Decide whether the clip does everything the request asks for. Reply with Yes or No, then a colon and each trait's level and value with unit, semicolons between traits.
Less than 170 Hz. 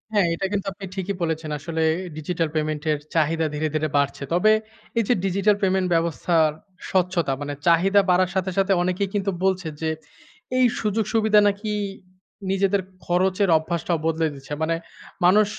No: medium, 180 Hz